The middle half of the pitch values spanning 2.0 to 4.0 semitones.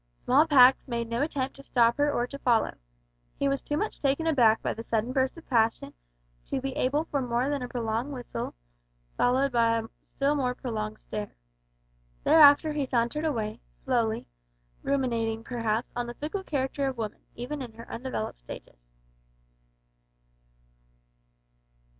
Yes: average, 3.4 semitones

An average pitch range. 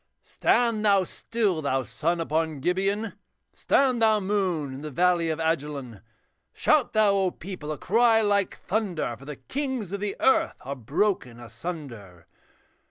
No: wide, 6.4 semitones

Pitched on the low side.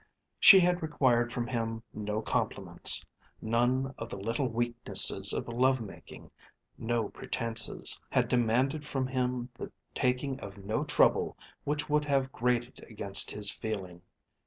Yes: low, 120 Hz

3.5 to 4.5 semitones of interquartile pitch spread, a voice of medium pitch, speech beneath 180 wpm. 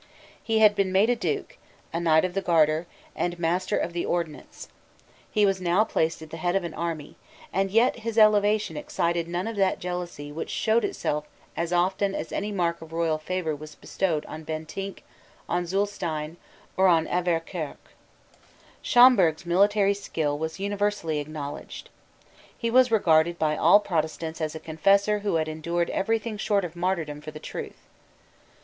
Yes: average, 4.1 semitones; medium, 175 Hz; average, 170 wpm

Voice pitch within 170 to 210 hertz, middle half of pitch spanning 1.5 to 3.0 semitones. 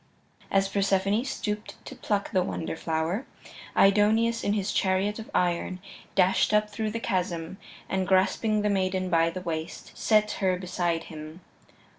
Yes: high, 190 Hz; average, 2.7 semitones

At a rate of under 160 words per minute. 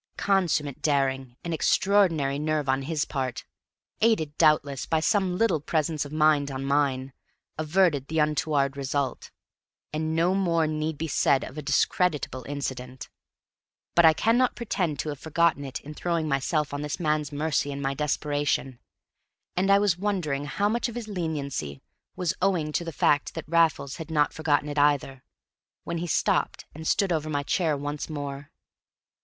No: average, 165 wpm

